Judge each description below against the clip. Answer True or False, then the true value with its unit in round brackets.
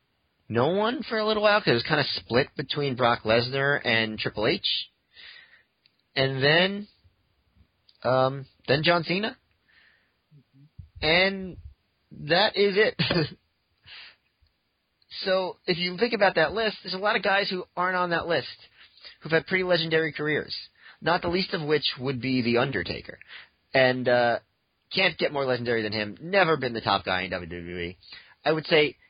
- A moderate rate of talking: True (160 wpm)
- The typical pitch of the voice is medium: True (145 Hz)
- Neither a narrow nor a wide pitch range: False (7.5 semitones)